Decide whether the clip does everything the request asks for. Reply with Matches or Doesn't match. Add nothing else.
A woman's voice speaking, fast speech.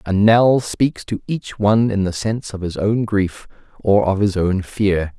Doesn't match